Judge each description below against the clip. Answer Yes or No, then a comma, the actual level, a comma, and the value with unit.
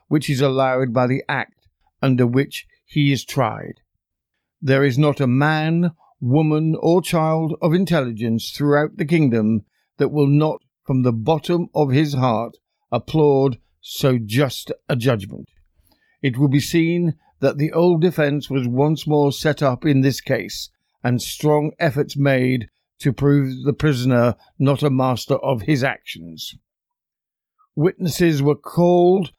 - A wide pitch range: No, average, 3.4 semitones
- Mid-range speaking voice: Yes, medium, 145 Hz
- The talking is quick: No, average, 145 wpm